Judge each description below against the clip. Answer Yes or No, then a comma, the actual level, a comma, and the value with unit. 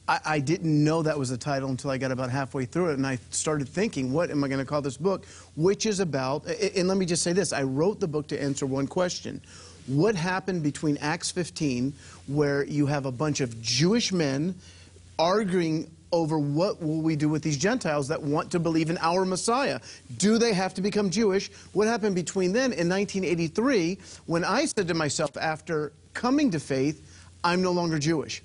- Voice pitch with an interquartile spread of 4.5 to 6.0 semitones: Yes, average, 4.8 semitones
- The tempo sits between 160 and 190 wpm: No, fast, 205 wpm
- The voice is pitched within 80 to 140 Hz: No, medium, 155 Hz